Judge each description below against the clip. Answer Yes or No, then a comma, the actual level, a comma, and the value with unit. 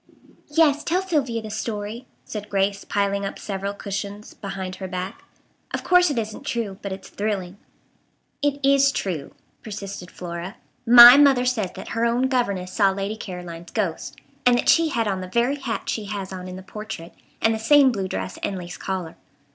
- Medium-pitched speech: No, high, 205 Hz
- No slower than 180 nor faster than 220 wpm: Yes, average, 185 wpm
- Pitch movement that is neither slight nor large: Yes, average, 4.3 semitones